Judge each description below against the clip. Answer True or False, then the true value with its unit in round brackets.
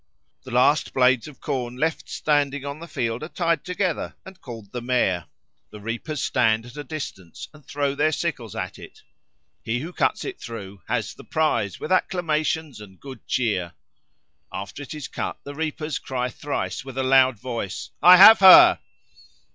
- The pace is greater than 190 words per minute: False (175 wpm)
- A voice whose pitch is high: False (135 Hz)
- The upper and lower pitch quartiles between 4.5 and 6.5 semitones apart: True (4.8 semitones)